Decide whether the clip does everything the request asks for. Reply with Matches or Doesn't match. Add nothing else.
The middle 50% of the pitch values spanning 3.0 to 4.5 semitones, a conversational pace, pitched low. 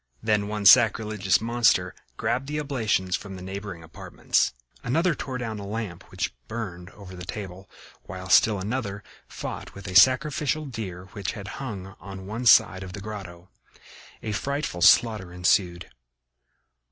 Matches